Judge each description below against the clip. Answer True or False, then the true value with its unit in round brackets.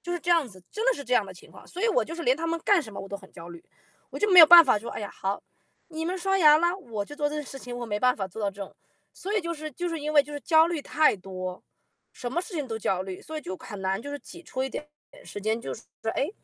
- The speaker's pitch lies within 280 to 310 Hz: True (285 Hz)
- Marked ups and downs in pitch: True (8.4 semitones)